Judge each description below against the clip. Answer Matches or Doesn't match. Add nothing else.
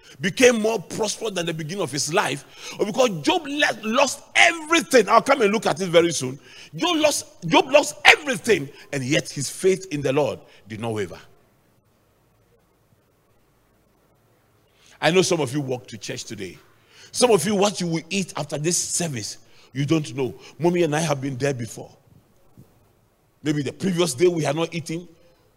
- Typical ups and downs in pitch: Doesn't match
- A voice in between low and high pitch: Matches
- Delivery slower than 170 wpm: Doesn't match